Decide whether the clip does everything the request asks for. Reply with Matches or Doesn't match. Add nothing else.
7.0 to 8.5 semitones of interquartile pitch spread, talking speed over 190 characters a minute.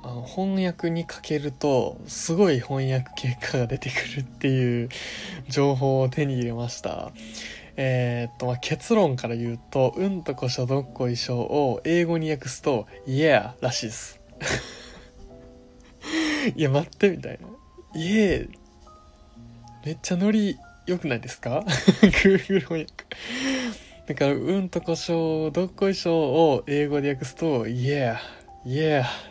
Doesn't match